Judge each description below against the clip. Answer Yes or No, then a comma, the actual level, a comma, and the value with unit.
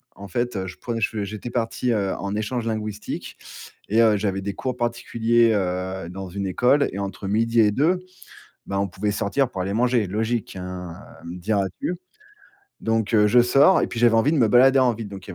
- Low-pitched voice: Yes, low, 110 Hz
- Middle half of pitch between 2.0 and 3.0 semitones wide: No, average, 3.4 semitones